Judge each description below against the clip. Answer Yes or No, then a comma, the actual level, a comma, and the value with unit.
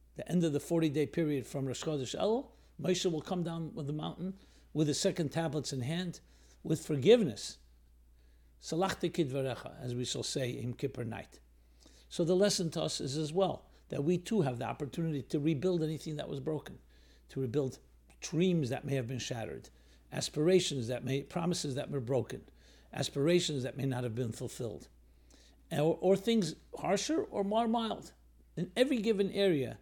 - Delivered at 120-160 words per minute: No, average, 175 wpm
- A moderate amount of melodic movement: No, wide, 6.0 semitones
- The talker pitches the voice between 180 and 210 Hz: No, medium, 145 Hz